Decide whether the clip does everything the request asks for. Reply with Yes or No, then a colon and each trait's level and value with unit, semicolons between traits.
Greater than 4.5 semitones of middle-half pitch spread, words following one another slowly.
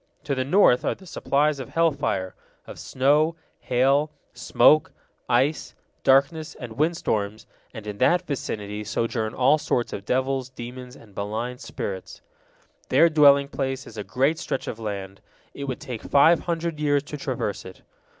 No: average, 4.9 semitones; average, 160 wpm